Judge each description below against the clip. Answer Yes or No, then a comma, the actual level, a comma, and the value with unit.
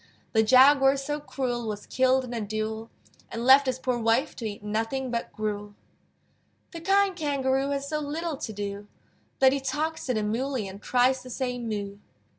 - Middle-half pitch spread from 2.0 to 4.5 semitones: Yes, average, 4.0 semitones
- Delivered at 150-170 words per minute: No, average, 185 wpm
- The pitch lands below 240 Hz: No, very high, 255 Hz